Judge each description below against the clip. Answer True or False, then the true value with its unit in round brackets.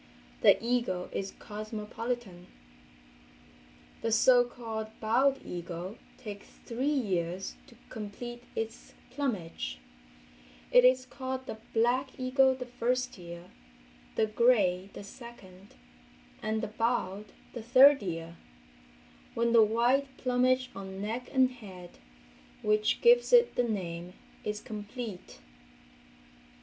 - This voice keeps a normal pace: False (115 wpm)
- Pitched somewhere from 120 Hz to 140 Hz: False (225 Hz)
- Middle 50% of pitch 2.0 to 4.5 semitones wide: True (4.2 semitones)